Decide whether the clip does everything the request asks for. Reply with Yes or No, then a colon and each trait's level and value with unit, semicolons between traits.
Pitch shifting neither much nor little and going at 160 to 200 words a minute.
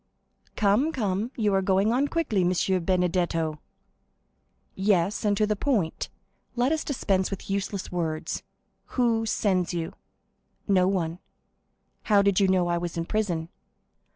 No: average, 3.3 semitones; average, 140 wpm